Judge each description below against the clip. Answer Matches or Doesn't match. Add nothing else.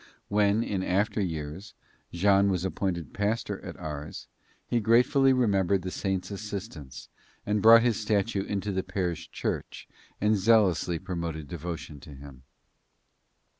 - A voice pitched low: Matches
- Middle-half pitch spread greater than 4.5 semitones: Doesn't match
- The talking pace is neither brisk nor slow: Doesn't match